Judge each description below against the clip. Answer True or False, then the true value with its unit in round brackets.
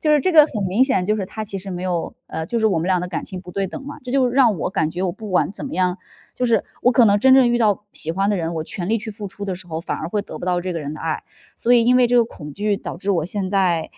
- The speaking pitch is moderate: False (200 Hz)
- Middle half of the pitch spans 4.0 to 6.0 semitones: True (4.6 semitones)